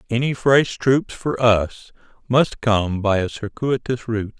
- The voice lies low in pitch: Yes, low, 120 Hz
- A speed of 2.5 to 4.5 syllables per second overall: Yes, 3.9 syllables/s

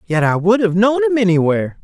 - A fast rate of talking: Yes, fast, 230 wpm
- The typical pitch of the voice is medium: Yes, medium, 170 Hz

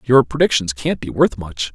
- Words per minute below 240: Yes, fast, 205 wpm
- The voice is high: No, low, 120 Hz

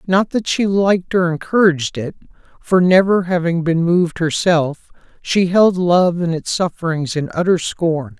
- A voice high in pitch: No, medium, 175 Hz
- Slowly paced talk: No, average, 160 wpm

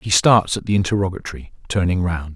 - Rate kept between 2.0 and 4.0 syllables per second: No, 6.0 syllables/s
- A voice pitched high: No, very low, 95 Hz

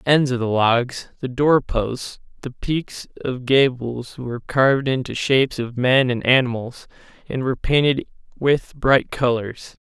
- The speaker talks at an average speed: Yes, average, 160 wpm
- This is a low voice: Yes, low, 130 Hz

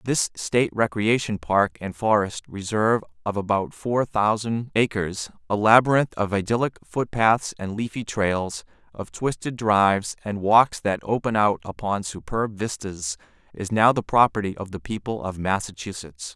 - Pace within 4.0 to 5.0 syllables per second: Yes, 4.5 syllables/s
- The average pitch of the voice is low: Yes, low, 105 Hz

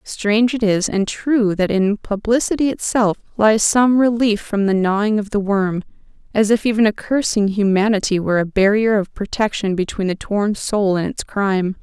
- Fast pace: No, average, 180 wpm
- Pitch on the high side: Yes, high, 210 Hz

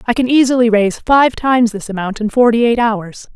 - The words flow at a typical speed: No, fast, 215 wpm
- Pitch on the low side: No, high, 230 Hz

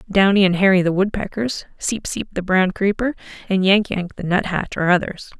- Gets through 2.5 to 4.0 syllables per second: No, 5.3 syllables/s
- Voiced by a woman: Yes, female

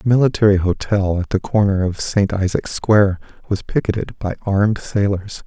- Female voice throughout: No, male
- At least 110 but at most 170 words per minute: Yes, average, 165 wpm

